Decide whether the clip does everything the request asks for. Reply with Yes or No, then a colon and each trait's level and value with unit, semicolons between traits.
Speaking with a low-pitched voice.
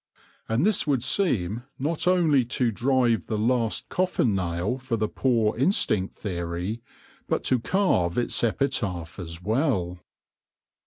Yes: low, 115 Hz